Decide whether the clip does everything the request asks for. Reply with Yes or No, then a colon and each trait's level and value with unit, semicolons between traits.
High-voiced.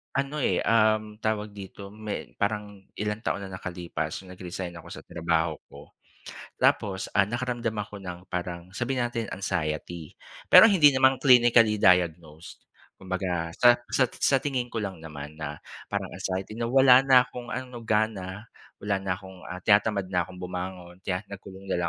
No: low, 100 Hz